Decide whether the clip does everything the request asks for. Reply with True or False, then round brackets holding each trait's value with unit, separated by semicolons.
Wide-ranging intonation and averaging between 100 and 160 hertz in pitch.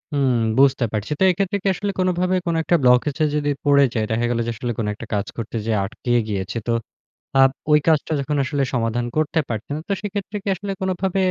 True (7.2 semitones; 140 Hz)